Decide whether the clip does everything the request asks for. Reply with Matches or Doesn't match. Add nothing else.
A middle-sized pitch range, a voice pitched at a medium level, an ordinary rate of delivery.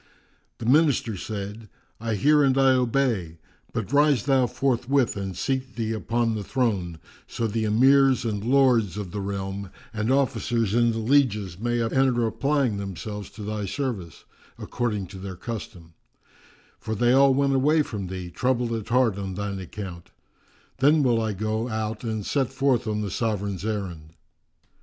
Doesn't match